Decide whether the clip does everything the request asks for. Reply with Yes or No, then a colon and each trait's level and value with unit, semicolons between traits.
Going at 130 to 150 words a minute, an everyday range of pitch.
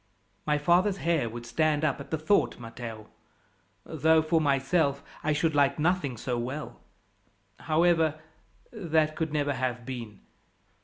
Yes: average, 140 wpm; average, 3.7 semitones